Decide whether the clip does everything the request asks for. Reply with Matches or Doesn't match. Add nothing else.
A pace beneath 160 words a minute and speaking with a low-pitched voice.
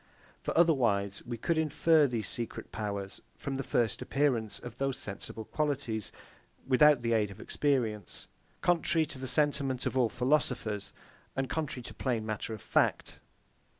Matches